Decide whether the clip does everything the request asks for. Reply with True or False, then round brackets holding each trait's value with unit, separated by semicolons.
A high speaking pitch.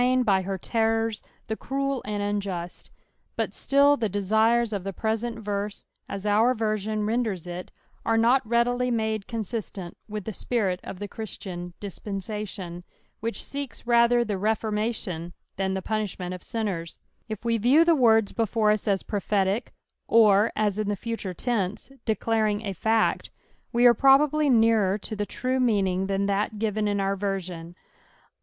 True (215 Hz)